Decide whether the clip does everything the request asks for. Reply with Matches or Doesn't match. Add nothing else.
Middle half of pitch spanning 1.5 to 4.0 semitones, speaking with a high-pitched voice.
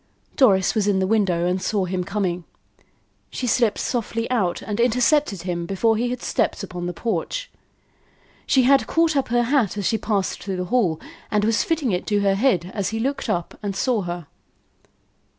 Doesn't match